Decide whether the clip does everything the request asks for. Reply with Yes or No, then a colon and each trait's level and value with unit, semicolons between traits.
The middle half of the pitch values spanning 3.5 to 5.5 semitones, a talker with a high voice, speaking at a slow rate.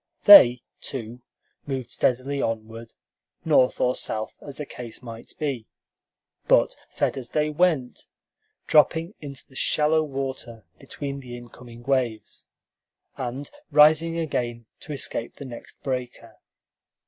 No: average, 3.8 semitones; low, 130 Hz; slow, 125 wpm